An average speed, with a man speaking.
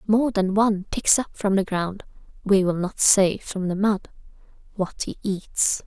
No: average, 165 wpm; female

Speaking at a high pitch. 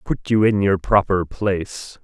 No: very low, 95 Hz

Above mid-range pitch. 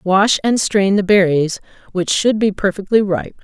Yes: high, 195 Hz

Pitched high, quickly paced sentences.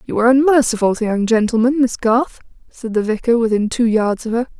Yes: high, 235 Hz; fast, 210 wpm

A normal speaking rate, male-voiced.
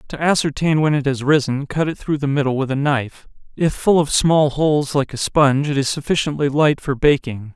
No: fast, 215 wpm; male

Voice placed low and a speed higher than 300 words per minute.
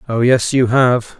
No: low, 125 Hz; average, 200 wpm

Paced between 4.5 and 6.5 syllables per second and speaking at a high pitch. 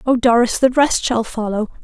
Yes: 5.0 syllables/s; high, 240 Hz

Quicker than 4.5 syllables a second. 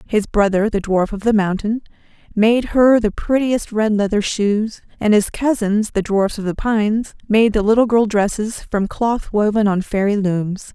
No: 4.4 syllables/s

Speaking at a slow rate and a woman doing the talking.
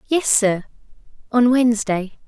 Yes: slow, 105 wpm; female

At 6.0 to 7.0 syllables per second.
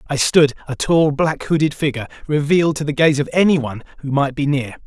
No: 5.8 syllables/s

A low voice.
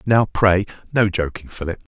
Yes: low, 100 Hz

